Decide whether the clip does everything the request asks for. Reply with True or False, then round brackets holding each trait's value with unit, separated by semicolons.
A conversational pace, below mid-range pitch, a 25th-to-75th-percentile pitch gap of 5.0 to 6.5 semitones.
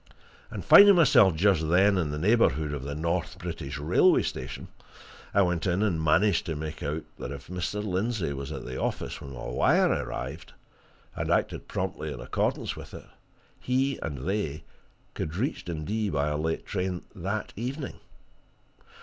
True (165 wpm; 85 Hz; 5.4 semitones)